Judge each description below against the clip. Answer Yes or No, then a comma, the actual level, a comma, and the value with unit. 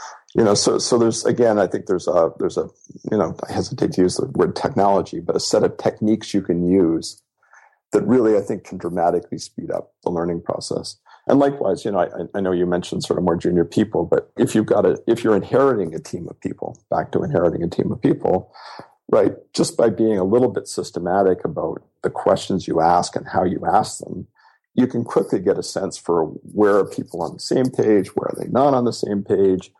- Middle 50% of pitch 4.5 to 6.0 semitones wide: No, average, 4.0 semitones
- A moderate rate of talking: No, fast, 230 wpm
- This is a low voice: Yes, very low, 95 Hz